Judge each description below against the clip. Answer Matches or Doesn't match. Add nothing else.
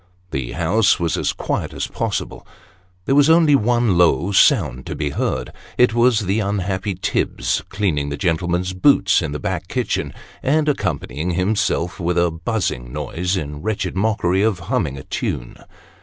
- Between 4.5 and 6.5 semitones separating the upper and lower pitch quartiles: Matches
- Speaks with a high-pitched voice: Doesn't match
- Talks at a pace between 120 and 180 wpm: Matches